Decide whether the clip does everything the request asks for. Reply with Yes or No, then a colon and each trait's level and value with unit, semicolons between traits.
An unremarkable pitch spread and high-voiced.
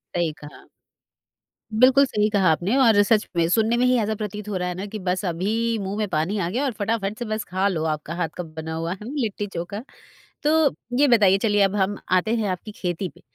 Yes: average, 3.6 semitones; high, 200 Hz